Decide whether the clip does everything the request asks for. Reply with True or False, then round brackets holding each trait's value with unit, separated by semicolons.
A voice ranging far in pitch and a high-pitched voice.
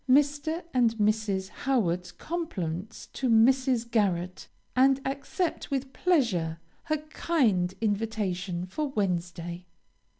True (6.9 semitones; 225 Hz)